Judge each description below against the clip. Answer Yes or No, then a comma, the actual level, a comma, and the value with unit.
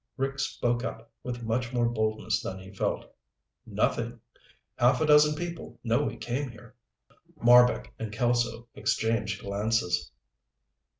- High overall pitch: No, low, 120 Hz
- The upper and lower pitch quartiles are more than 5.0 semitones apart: No, narrow, 2.4 semitones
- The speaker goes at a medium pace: No, slow, 130 wpm